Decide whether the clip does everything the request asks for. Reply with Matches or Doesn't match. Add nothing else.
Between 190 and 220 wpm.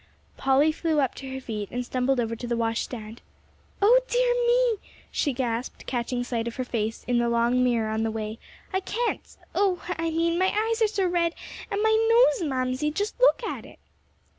Matches